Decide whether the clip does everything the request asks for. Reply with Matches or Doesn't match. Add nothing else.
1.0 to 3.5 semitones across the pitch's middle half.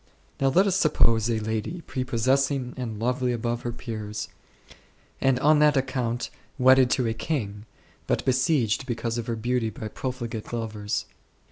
Matches